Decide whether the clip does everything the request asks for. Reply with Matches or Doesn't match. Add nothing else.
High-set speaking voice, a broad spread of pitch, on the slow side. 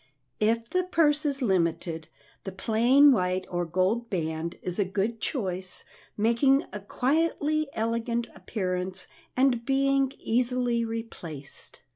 Matches